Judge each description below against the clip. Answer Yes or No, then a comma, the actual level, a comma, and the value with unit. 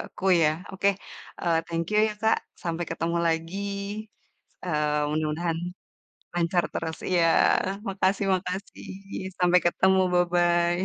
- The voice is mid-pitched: Yes, medium, 175 Hz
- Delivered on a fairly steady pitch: Yes, narrow, 1.9 semitones